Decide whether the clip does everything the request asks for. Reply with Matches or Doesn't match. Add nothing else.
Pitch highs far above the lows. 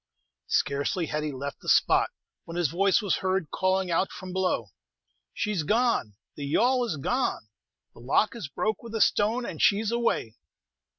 Matches